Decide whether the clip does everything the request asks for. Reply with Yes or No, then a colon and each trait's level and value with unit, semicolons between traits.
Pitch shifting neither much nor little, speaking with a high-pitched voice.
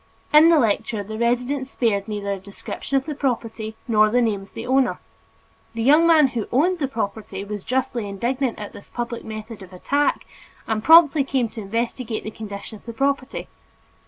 Yes: average, 4.1 semitones; high, 235 Hz